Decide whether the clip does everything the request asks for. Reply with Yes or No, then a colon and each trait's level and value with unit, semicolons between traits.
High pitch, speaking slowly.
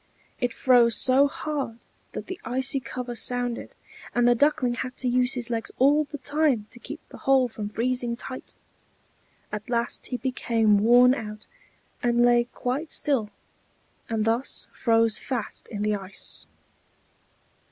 No: high, 245 Hz; average, 150 wpm